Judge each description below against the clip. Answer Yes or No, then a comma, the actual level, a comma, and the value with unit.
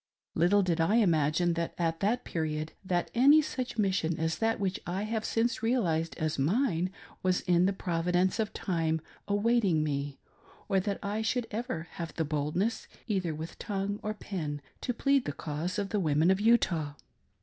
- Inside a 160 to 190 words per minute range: Yes, average, 175 wpm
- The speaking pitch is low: No, medium, 185 Hz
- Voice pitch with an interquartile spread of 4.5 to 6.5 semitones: Yes, average, 4.8 semitones